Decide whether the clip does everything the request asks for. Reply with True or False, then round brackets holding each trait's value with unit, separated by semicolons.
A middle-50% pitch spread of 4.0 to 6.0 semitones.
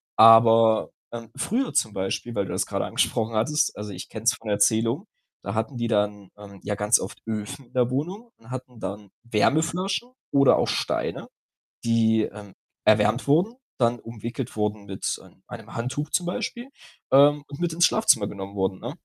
True (5.1 semitones)